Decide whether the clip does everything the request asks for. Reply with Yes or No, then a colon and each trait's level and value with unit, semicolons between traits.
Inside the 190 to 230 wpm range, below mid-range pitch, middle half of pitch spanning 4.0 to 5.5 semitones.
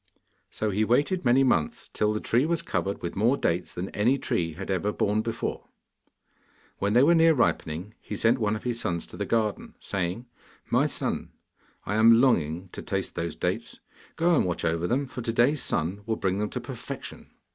Yes: average, 200 wpm; low, 105 Hz; average, 5.2 semitones